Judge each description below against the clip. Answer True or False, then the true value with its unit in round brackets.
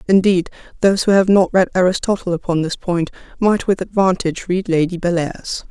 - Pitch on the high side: False (180 Hz)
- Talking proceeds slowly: False (170 wpm)